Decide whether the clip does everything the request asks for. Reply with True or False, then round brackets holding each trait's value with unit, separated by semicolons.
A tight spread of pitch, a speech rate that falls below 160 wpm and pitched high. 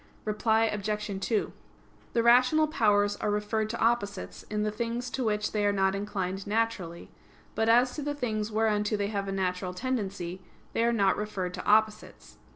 False (2.2 semitones; 175 wpm; 210 Hz)